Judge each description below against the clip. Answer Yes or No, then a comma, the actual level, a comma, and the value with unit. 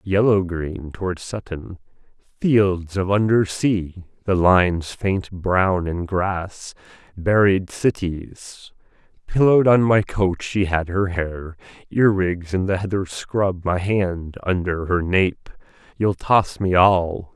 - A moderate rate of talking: No, slow, 125 wpm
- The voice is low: Yes, very low, 95 Hz